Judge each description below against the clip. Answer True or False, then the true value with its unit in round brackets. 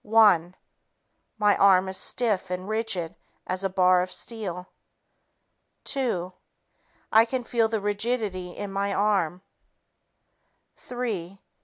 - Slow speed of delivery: True (115 wpm)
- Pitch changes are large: False (3.3 semitones)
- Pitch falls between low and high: False (200 Hz)